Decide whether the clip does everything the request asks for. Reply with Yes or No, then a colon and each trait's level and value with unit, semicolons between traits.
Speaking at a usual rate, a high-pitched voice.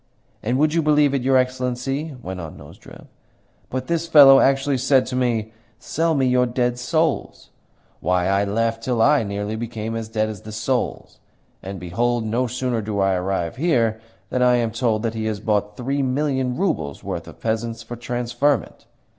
No: average, 180 wpm; low, 120 Hz